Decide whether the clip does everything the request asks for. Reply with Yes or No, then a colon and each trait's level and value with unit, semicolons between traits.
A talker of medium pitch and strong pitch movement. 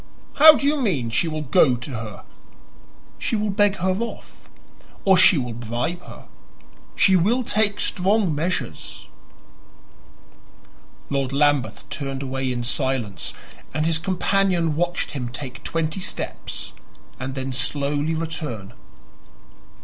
Yes: medium, 155 Hz; wide, 6.2 semitones